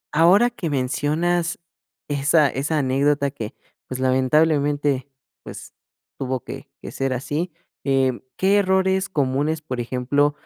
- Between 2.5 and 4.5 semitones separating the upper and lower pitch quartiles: Yes, average, 3.6 semitones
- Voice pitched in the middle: Yes, medium, 145 Hz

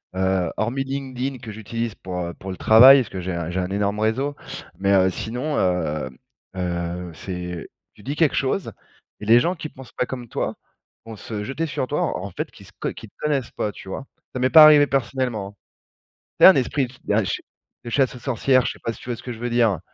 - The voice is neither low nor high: No, low, 115 Hz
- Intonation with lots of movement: Yes, wide, 5.7 semitones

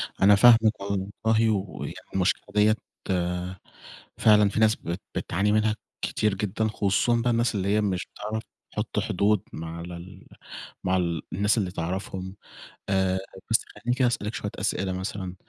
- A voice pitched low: Yes, low, 100 Hz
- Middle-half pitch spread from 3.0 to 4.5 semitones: No, narrow, 2.4 semitones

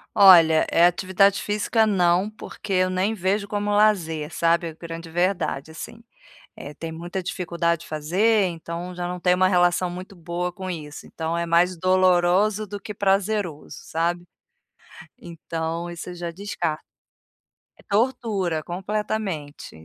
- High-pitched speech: No, medium, 180 Hz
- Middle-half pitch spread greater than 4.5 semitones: No, average, 2.9 semitones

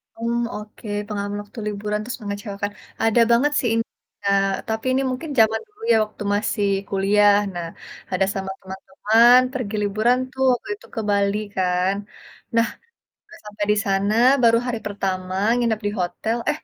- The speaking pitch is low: No, high, 210 Hz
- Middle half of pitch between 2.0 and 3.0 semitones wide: Yes, narrow, 2.6 semitones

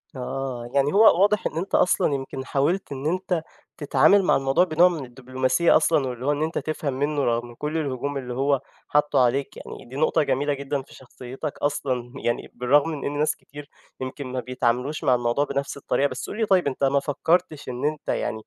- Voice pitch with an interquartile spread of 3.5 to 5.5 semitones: No, average, 3.0 semitones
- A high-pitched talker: No, medium, 140 Hz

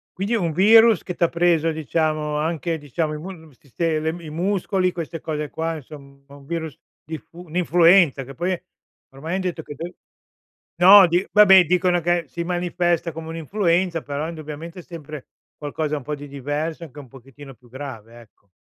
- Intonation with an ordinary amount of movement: Yes, average, 3.1 semitones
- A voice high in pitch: No, medium, 160 Hz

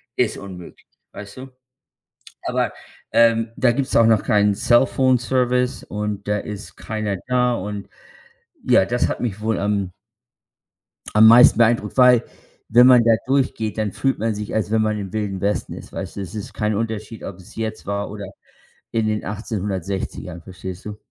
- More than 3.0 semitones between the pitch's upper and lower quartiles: No, average, 2.7 semitones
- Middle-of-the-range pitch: No, low, 110 Hz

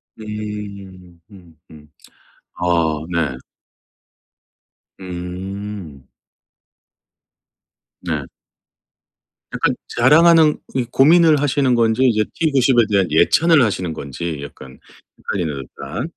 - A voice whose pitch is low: Yes, low, 100 Hz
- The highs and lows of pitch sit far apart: Yes, wide, 7.2 semitones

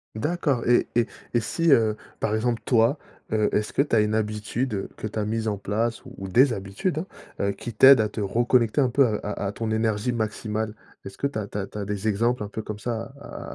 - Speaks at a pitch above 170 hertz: No, low, 110 Hz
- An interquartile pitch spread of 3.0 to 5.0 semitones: No, narrow, 2.5 semitones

